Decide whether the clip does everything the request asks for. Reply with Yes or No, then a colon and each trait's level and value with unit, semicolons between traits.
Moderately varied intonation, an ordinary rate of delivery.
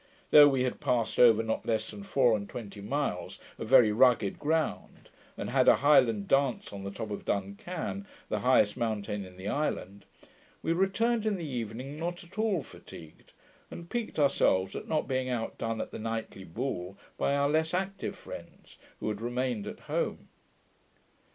No: wide, 6.4 semitones; average, 175 wpm